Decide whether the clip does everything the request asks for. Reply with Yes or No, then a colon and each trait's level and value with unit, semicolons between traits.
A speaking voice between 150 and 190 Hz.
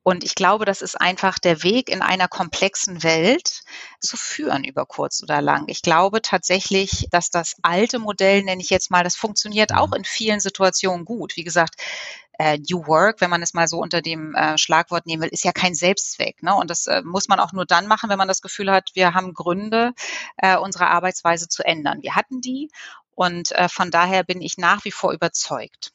Yes: medium, 185 Hz